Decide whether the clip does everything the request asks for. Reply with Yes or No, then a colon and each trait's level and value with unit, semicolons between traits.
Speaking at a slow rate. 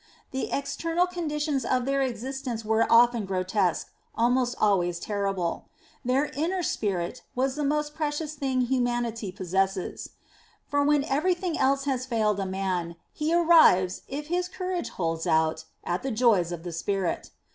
No: average, 145 wpm